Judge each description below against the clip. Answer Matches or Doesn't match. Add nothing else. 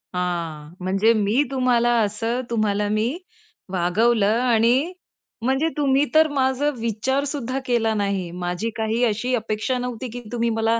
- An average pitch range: Matches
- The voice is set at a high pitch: Matches